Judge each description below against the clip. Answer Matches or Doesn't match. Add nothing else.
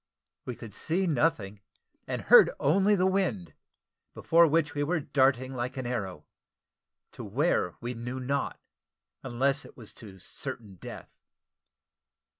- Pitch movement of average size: Doesn't match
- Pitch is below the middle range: Matches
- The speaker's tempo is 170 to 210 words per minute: Doesn't match